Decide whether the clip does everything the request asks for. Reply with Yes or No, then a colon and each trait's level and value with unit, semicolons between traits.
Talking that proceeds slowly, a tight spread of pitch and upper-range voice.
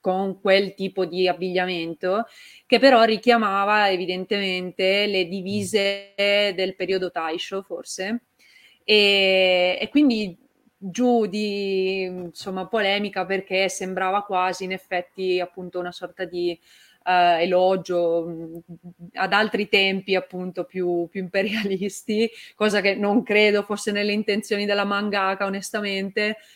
Yes: slow, 110 wpm; narrow, 2.0 semitones; high, 195 Hz